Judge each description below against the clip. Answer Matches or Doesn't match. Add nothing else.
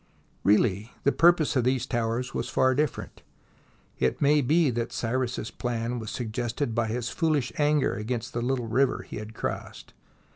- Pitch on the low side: Matches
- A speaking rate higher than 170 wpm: Doesn't match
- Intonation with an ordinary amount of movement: Matches